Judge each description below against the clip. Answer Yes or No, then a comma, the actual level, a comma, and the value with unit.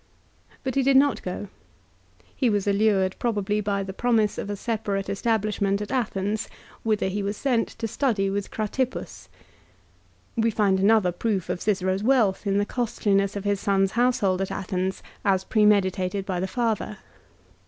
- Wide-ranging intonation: No, narrow, 2.4 semitones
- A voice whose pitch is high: Yes, high, 205 Hz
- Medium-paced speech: Yes, average, 160 wpm